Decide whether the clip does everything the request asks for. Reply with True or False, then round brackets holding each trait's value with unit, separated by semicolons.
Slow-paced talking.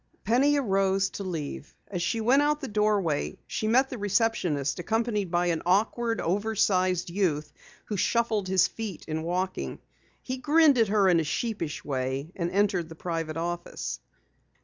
False (160 wpm)